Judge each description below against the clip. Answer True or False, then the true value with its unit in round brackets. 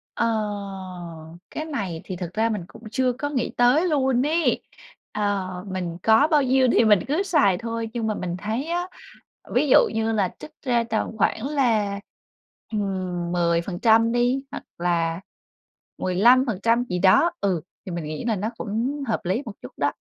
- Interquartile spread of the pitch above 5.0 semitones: True (5.6 semitones)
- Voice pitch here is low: False (225 Hz)